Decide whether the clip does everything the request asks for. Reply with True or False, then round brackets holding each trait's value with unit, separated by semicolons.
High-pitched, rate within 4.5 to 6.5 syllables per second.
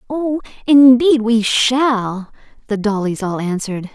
False (230 Hz; 3.9 syllables/s)